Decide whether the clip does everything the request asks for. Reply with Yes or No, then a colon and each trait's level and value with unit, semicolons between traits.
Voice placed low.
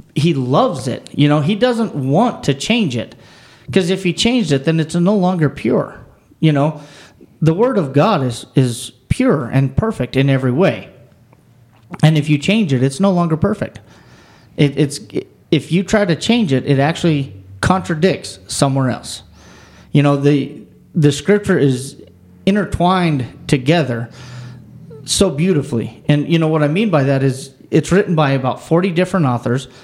No: medium, 145 Hz